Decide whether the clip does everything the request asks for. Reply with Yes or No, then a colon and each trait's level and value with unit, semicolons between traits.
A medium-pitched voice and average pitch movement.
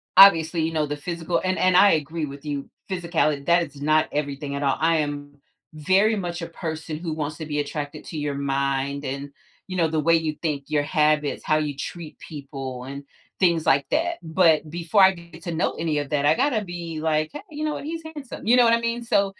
Yes: medium, 160 Hz; average, 3.3 semitones